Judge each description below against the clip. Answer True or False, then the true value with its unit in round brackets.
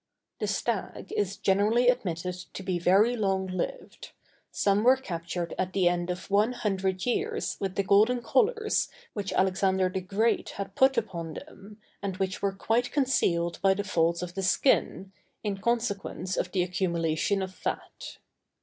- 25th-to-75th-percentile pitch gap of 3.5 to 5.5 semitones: False (3.0 semitones)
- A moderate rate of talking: True (160 wpm)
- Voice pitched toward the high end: True (195 Hz)